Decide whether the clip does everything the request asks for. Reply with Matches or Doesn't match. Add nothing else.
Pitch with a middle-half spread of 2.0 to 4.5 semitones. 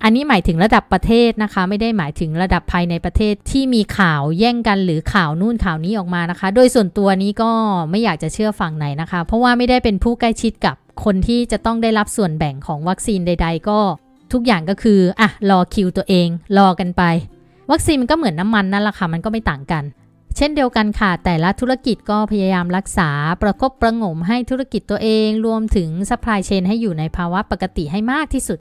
Matches